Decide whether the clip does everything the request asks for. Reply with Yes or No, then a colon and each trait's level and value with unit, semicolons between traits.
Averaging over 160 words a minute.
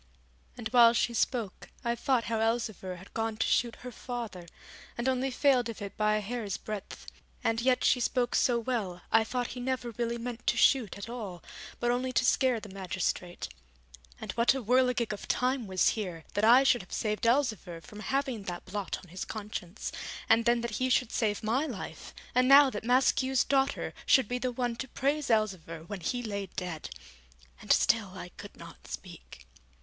Yes: average, 195 wpm